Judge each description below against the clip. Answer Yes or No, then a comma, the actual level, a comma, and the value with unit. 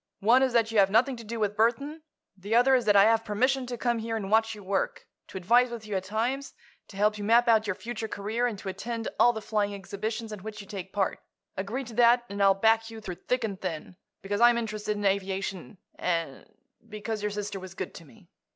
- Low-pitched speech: No, high, 215 Hz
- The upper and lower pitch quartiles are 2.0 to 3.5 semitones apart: Yes, average, 2.8 semitones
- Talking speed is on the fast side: Yes, fast, 235 wpm